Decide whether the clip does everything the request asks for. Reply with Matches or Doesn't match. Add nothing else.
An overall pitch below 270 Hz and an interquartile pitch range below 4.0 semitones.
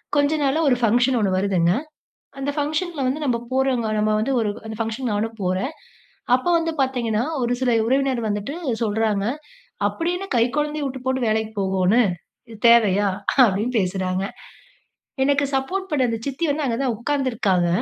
Doesn't match